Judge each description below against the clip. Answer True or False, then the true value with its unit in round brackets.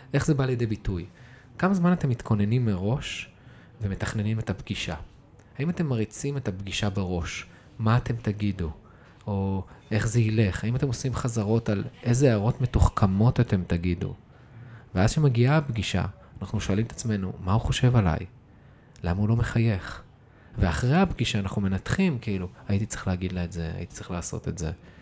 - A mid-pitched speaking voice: False (110 Hz)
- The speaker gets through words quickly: True (160 wpm)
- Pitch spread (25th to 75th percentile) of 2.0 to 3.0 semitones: False (4.3 semitones)